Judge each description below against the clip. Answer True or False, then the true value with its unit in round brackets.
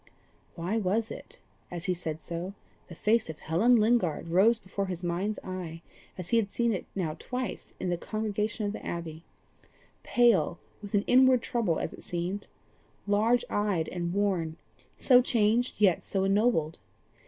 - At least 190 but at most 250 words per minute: False (165 wpm)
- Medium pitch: False (195 Hz)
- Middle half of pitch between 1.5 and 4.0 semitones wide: False (4.5 semitones)